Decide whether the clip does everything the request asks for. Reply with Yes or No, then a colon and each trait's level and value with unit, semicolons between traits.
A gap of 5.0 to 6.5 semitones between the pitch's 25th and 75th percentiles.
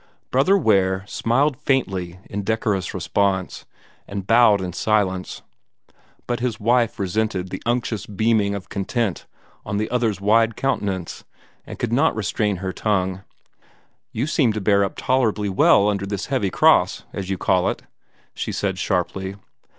No: average, 3.2 semitones